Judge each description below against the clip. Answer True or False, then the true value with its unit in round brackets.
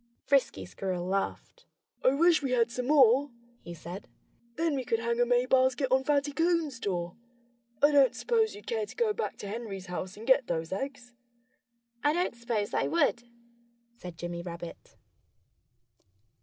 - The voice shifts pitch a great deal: True (6.4 semitones)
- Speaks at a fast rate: False (165 wpm)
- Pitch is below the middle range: False (245 Hz)